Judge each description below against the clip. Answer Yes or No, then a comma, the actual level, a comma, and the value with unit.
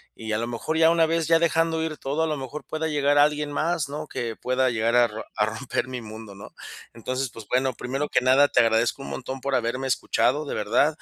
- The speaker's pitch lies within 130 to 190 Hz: Yes, low, 135 Hz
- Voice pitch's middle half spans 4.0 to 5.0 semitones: Yes, average, 4.4 semitones